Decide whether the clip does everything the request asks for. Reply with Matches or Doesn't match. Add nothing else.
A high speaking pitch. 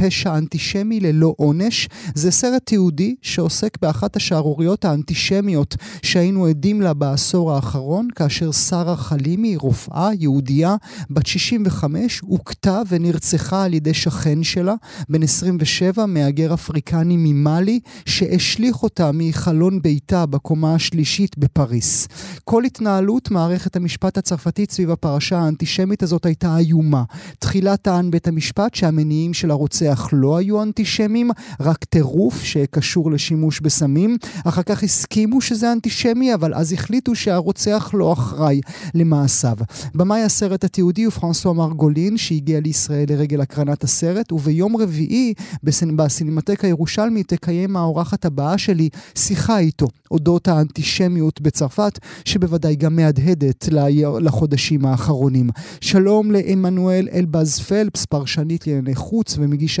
Doesn't match